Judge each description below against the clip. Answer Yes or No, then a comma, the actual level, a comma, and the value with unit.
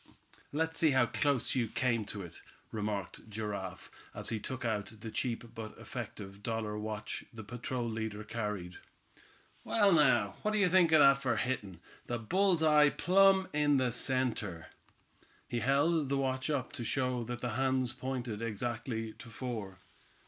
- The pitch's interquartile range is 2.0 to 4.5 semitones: Yes, average, 4.1 semitones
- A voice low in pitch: Yes, low, 120 Hz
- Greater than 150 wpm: Yes, average, 160 wpm